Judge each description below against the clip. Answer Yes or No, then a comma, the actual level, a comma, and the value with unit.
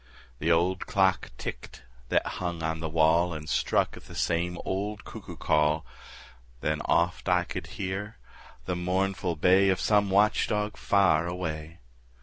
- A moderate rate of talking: Yes, average, 150 wpm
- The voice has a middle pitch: No, very low, 90 Hz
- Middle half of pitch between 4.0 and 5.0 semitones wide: No, average, 3.0 semitones